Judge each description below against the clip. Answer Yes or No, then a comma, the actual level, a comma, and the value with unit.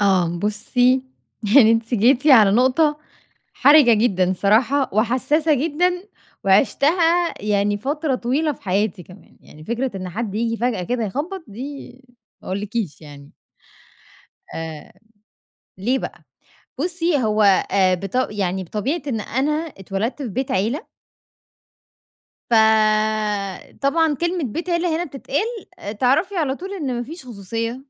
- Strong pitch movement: Yes, wide, 6.3 semitones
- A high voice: Yes, high, 240 Hz